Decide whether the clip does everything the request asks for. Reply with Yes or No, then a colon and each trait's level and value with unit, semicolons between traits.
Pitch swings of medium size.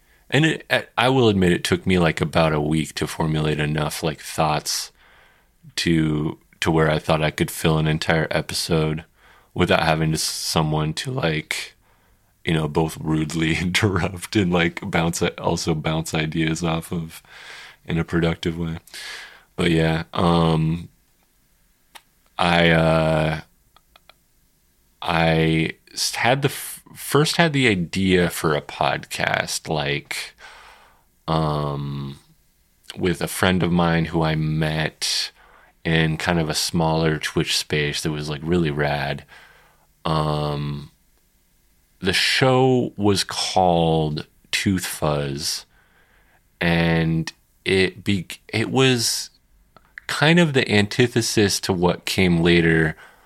No: narrow, 2.3 semitones